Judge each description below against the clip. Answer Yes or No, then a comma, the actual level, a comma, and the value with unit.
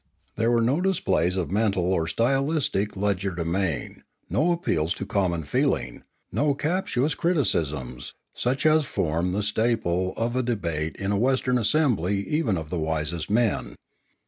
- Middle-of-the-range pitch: No, low, 100 Hz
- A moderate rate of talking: Yes, average, 145 wpm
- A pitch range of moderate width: No, wide, 7.0 semitones